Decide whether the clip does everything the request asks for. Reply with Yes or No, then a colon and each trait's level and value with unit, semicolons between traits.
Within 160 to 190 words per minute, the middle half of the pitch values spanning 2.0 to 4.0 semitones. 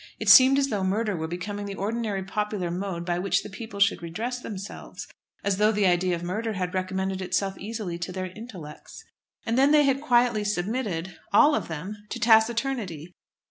Yes: average, 185 wpm; average, 3.7 semitones